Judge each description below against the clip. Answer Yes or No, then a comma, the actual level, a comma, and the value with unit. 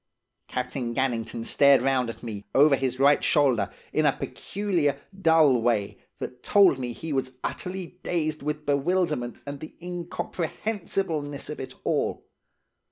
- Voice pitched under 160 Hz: Yes, medium, 140 Hz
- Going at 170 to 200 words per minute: No, average, 140 wpm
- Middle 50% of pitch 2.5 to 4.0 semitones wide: No, average, 4.6 semitones